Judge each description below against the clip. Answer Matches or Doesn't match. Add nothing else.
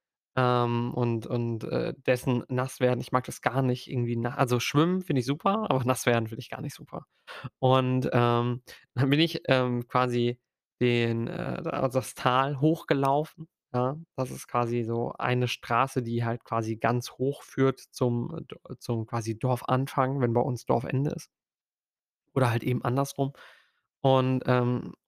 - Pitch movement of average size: Doesn't match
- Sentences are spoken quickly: Doesn't match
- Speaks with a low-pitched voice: Matches